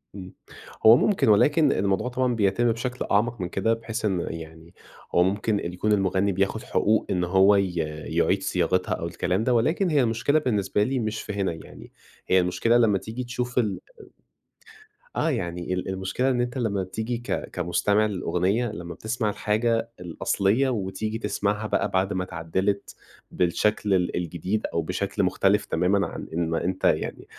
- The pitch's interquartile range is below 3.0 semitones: No, average, 3.8 semitones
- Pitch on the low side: Yes, low, 100 Hz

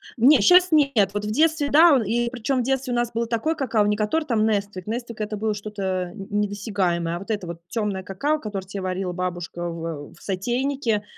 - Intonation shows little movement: No, average, 4.4 semitones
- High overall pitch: Yes, high, 215 Hz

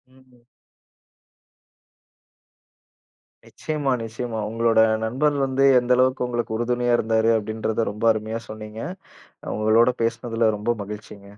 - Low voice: Yes, low, 115 Hz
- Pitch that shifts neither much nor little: No, narrow, 2.0 semitones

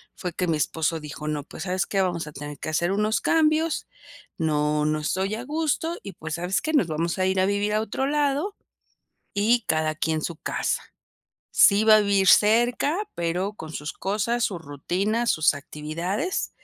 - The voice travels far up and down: Yes, wide, 5.8 semitones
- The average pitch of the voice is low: No, high, 190 Hz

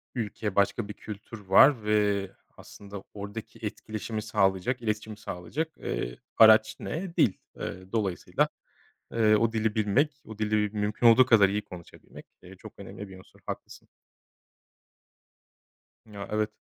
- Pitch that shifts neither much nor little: No, narrow, 2.0 semitones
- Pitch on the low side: Yes, low, 105 Hz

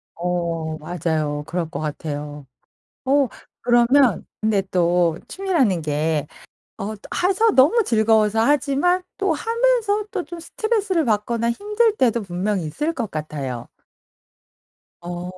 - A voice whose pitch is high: Yes, high, 220 Hz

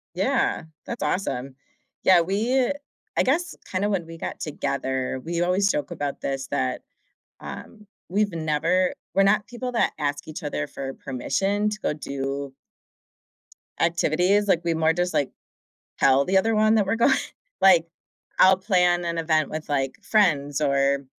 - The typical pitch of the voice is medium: Yes, medium, 170 Hz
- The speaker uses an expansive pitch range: Yes, wide, 5.8 semitones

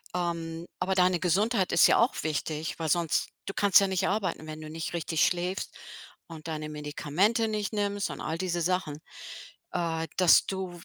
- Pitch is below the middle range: No, medium, 175 Hz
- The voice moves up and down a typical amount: Yes, average, 3.0 semitones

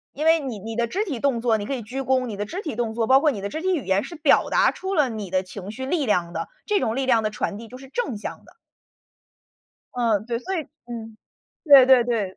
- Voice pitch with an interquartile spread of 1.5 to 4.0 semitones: No, average, 4.6 semitones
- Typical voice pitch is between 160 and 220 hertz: No, high, 240 Hz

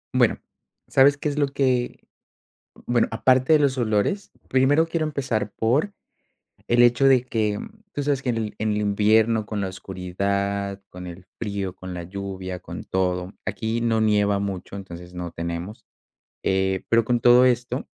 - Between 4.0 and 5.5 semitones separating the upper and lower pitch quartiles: Yes, average, 4.7 semitones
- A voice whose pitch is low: Yes, low, 110 Hz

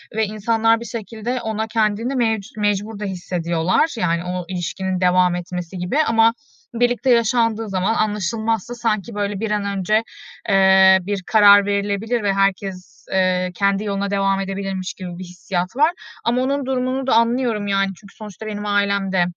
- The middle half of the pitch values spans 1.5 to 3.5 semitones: Yes, average, 3.0 semitones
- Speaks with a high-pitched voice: Yes, high, 205 Hz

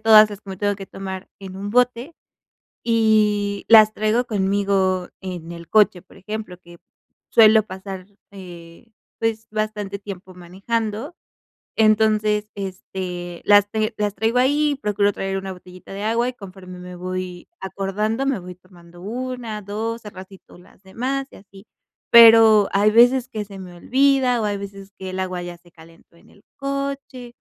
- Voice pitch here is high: Yes, high, 205 Hz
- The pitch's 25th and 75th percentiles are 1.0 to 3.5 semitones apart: Yes, average, 3.1 semitones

